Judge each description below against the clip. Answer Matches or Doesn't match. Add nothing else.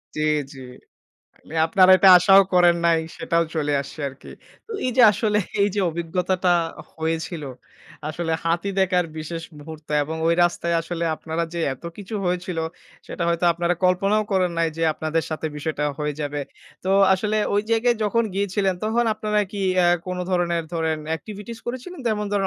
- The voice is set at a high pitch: Doesn't match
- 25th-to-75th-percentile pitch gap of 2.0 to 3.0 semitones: Doesn't match